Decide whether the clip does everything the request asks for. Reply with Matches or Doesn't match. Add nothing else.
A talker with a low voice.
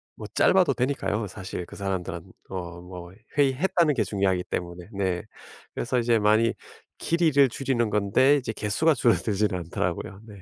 Matches